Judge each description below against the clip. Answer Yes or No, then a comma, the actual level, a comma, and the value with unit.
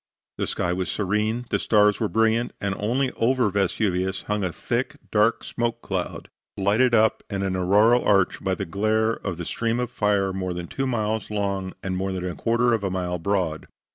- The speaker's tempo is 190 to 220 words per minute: Yes, average, 200 wpm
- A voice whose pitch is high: No, low, 105 Hz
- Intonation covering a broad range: No, average, 3.3 semitones